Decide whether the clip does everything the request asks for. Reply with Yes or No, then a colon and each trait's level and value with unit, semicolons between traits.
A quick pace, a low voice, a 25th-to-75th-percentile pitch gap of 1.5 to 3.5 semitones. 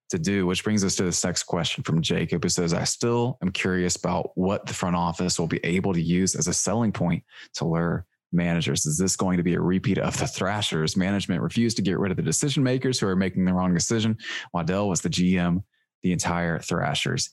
Yes: fast, 230 wpm; very low, 90 Hz; average, 2.9 semitones